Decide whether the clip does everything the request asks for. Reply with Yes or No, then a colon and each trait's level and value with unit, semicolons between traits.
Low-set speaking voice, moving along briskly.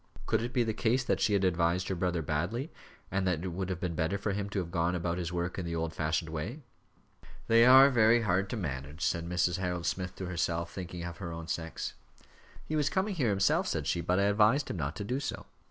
Yes: very low, 90 Hz; fast, 245 wpm